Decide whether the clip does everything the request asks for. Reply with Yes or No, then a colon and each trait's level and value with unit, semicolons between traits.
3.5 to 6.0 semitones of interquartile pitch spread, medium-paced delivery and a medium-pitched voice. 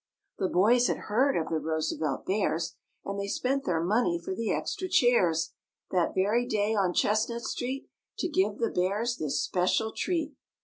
No: average, 5.3 semitones; average, 170 wpm; high, 205 Hz